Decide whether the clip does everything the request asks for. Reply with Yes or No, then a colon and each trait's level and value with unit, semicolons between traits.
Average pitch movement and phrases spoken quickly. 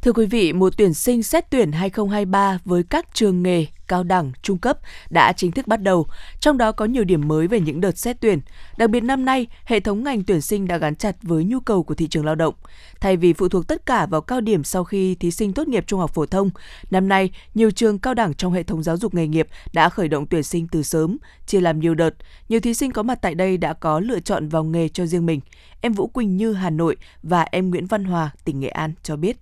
Yes: average, 5.0 semitones; fast, 260 wpm